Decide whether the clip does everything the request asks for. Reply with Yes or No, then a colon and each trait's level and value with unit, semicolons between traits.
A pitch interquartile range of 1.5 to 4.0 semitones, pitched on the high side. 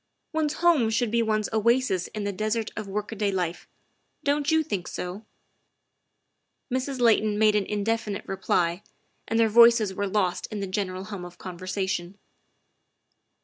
Yes: average, 3.2 semitones; high, 210 Hz